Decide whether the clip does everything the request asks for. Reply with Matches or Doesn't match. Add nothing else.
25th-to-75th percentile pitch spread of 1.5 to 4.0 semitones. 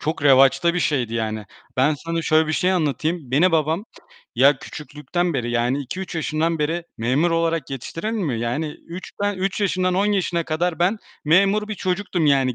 Doesn't match